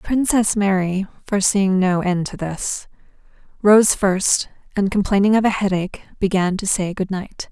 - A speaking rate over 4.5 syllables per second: Yes, 4.7 syllables/s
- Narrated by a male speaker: No, female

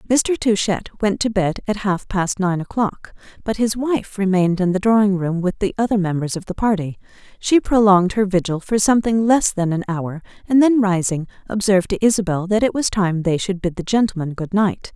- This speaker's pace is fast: Yes, fast, 210 wpm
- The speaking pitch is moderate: No, high, 195 Hz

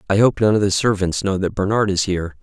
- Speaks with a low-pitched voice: Yes, low, 100 Hz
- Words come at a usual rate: No, fast, 275 wpm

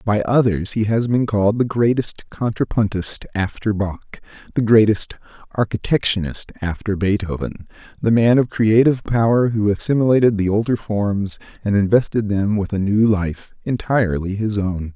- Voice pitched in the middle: No, low, 105 Hz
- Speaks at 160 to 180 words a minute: No, average, 145 wpm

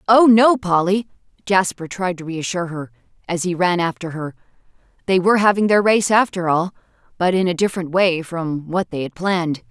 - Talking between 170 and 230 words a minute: Yes, average, 185 wpm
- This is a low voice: No, medium, 180 Hz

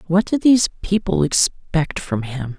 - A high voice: No, medium, 165 Hz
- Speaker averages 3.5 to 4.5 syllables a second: Yes, 4.4 syllables/s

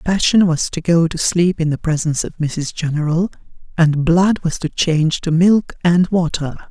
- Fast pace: No, average, 190 wpm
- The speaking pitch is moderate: Yes, medium, 165 Hz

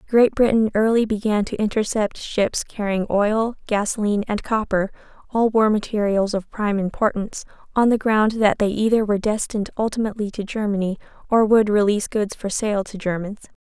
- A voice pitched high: Yes, high, 210 Hz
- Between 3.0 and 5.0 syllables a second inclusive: No, 5.5 syllables/s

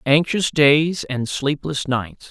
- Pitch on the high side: No, medium, 150 Hz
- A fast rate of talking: No, slow, 130 wpm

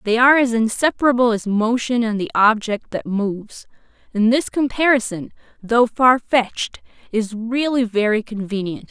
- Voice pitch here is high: Yes, high, 230 Hz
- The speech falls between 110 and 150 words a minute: Yes, average, 140 wpm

